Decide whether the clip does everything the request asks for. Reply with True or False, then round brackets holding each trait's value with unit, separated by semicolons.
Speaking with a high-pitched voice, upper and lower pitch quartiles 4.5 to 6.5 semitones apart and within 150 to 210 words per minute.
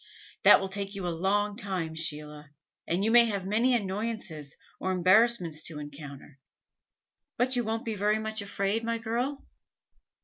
True (200 Hz; 5.2 semitones; 160 wpm)